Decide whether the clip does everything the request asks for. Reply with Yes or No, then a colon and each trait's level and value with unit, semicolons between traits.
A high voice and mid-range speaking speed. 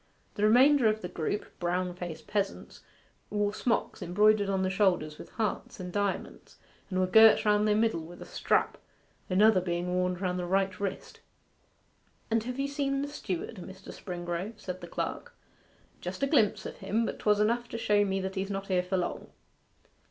Yes: high, 195 Hz; average, 190 wpm